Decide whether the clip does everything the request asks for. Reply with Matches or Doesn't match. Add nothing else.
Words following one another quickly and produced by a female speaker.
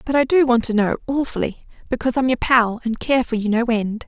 Matches